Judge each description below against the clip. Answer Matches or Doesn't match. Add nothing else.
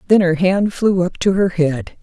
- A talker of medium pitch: Matches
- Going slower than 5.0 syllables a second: Matches